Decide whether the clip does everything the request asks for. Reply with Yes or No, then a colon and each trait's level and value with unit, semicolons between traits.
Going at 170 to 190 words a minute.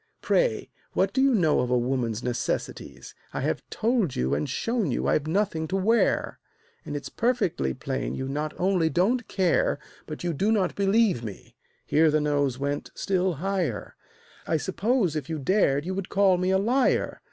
Yes: average, 180 wpm